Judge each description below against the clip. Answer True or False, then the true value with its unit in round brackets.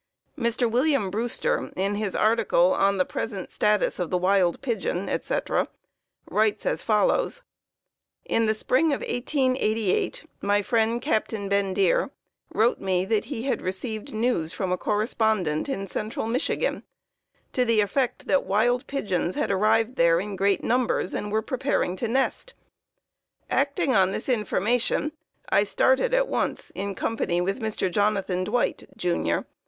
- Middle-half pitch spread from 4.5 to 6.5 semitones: False (4.0 semitones)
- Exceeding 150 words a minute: False (145 wpm)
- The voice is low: False (215 Hz)